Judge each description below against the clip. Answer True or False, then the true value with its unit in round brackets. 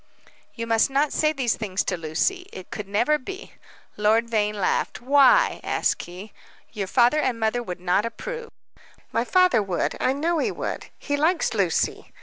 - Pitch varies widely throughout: True (6.7 semitones)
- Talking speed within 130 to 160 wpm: False (170 wpm)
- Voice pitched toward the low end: False (230 Hz)